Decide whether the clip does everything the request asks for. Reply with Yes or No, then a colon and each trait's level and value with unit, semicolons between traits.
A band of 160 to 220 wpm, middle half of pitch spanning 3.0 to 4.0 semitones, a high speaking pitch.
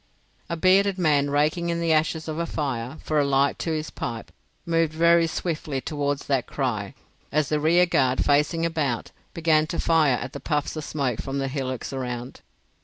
No: average, 180 wpm; average, 3.4 semitones; medium, 150 Hz